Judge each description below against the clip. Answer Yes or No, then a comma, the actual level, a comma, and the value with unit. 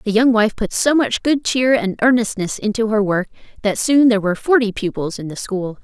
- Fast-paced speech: Yes, fast, 225 wpm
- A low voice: No, high, 220 Hz